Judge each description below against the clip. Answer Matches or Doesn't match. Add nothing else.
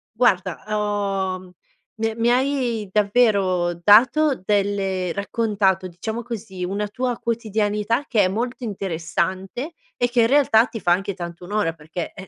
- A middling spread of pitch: Matches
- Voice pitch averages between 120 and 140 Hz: Doesn't match